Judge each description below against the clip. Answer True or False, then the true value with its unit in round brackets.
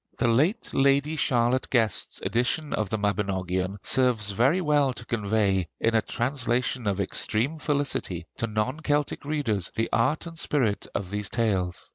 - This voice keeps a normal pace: True (155 wpm)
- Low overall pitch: True (115 Hz)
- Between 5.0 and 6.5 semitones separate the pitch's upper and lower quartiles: True (5.3 semitones)